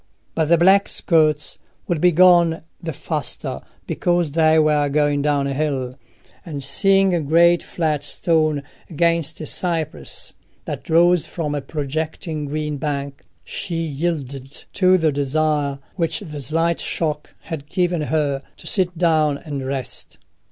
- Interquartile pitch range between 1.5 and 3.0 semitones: Yes, average, 2.7 semitones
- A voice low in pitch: No, medium, 155 Hz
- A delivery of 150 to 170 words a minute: No, average, 140 wpm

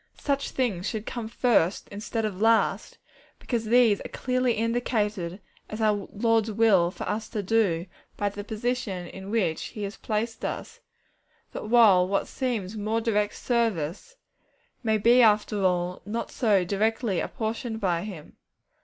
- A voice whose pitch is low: No, high, 215 Hz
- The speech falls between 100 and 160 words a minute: Yes, average, 145 wpm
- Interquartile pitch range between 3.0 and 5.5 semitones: No, narrow, 2.6 semitones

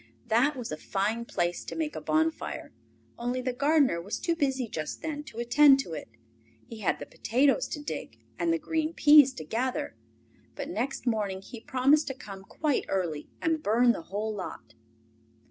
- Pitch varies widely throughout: Yes, wide, 6.2 semitones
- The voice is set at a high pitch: Yes, very high, 250 Hz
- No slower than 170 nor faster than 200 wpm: Yes, average, 180 wpm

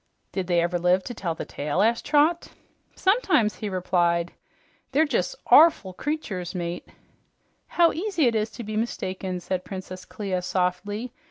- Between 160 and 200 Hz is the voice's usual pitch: Yes, high, 190 Hz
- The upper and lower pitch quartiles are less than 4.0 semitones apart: No, wide, 5.4 semitones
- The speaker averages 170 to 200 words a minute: No, average, 155 wpm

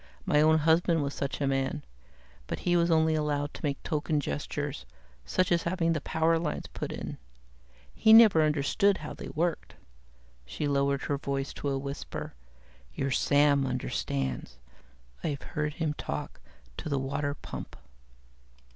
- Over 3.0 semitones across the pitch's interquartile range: No, narrow, 2.6 semitones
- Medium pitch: Yes, medium, 150 Hz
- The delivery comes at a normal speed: Yes, average, 155 wpm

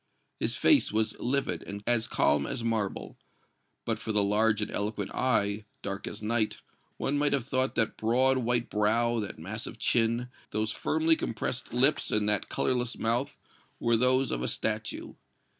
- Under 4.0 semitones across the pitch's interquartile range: Yes, average, 3.0 semitones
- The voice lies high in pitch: No, low, 115 Hz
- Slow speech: No, average, 165 wpm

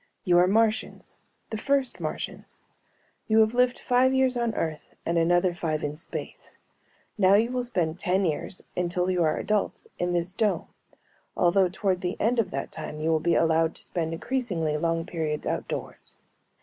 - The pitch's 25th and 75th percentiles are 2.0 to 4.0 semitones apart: No, average, 4.9 semitones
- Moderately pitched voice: Yes, medium, 180 Hz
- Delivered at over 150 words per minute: Yes, average, 175 wpm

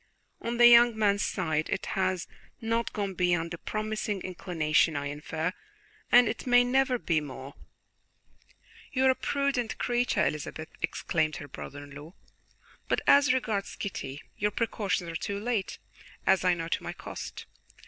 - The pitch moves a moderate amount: No, wide, 6.7 semitones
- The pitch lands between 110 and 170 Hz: No, high, 195 Hz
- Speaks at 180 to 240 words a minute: No, average, 160 wpm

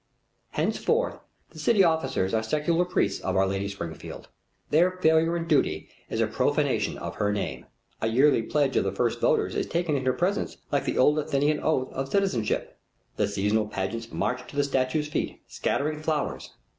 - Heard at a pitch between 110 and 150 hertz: Yes, medium, 140 Hz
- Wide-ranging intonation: Yes, wide, 6.4 semitones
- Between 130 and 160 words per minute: No, average, 180 wpm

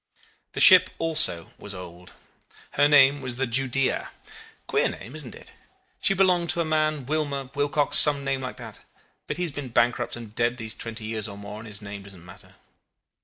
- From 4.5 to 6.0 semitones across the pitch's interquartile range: Yes, average, 5.1 semitones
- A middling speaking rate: Yes, average, 190 wpm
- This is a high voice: No, low, 130 Hz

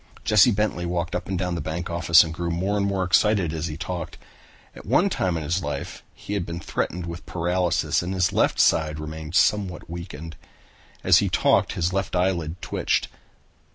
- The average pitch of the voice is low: Yes, very low, 85 Hz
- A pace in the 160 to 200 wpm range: Yes, average, 195 wpm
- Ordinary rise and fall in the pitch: No, narrow, 2.0 semitones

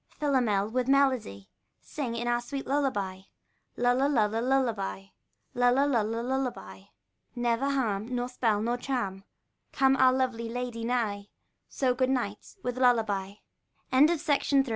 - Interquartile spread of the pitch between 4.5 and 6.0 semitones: No, average, 3.5 semitones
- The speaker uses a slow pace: Yes, slow, 120 wpm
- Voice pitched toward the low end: No, high, 245 Hz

